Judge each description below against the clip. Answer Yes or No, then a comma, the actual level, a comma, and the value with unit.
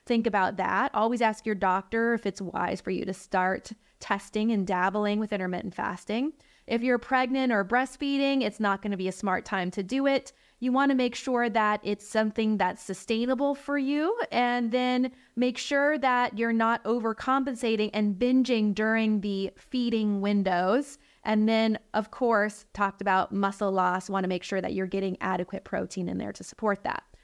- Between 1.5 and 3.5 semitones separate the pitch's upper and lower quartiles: No, average, 3.9 semitones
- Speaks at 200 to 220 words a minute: No, average, 185 wpm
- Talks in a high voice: Yes, high, 220 Hz